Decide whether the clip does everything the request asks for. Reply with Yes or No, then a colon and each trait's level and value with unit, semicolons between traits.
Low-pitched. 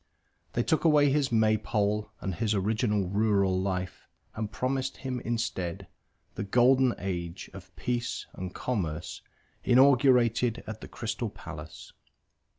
Yes: low, 110 Hz